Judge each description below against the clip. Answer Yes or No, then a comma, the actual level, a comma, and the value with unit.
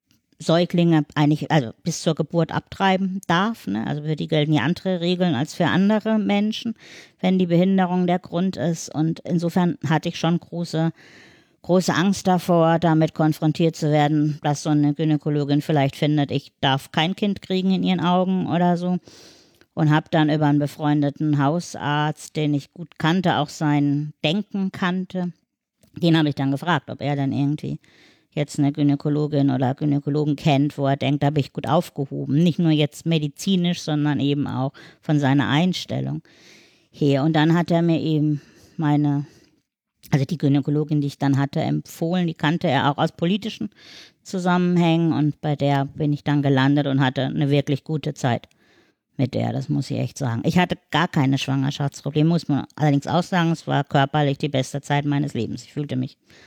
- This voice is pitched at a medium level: Yes, medium, 150 Hz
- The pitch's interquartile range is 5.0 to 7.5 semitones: No, average, 3.1 semitones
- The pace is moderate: Yes, average, 175 wpm